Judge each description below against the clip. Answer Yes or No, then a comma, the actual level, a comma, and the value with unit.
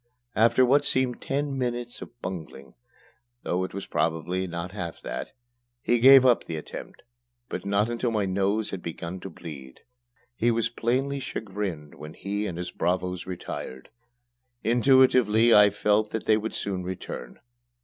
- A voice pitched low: Yes, low, 105 Hz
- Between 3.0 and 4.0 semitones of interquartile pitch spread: No, average, 4.9 semitones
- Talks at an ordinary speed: Yes, average, 155 wpm